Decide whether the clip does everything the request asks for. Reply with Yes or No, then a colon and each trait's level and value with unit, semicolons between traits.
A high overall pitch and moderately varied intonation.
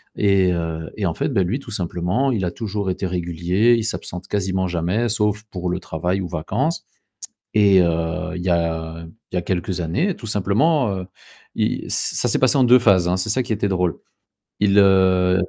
No: very low, 95 Hz; average, 3.2 semitones